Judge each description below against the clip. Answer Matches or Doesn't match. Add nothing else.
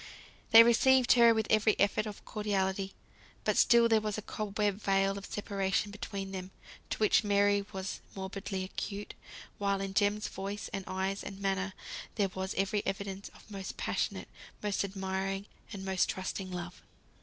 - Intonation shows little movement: Matches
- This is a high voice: Matches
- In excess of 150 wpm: Matches